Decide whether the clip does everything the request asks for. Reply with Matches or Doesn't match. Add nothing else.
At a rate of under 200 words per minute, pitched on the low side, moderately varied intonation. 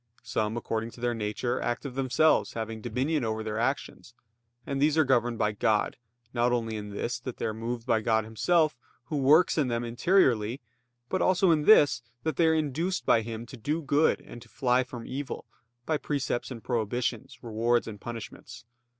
Matches